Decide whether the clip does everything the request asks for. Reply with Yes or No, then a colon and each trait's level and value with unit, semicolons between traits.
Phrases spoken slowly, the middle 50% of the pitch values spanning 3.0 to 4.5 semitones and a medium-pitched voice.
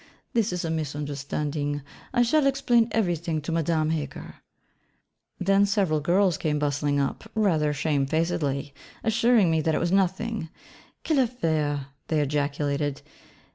No: slow, 130 wpm; average, 5.3 semitones; medium, 160 Hz